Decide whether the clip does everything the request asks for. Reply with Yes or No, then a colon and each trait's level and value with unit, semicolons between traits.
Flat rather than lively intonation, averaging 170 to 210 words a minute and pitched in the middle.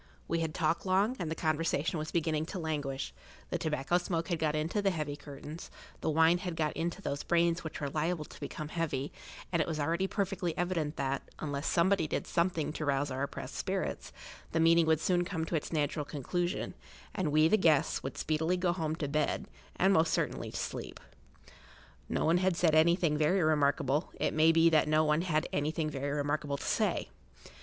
Yes: narrow, 2.3 semitones; average, 200 wpm; medium, 160 Hz